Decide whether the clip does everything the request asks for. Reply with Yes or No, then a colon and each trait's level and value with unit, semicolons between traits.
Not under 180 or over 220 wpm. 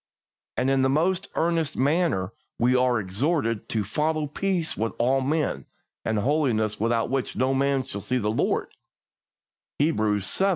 No: average, 155 wpm